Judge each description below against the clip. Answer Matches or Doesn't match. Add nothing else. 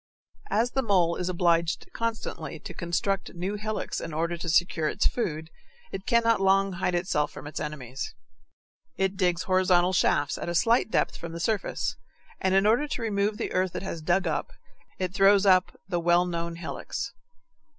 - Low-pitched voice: Doesn't match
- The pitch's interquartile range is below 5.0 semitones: Matches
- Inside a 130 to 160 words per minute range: Doesn't match